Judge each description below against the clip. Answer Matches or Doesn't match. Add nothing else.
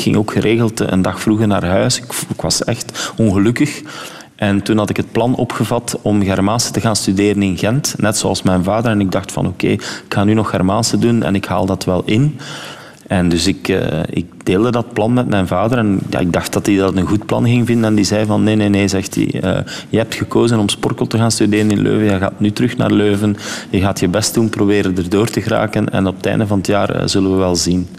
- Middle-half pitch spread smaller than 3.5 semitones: Matches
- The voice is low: Matches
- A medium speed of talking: Doesn't match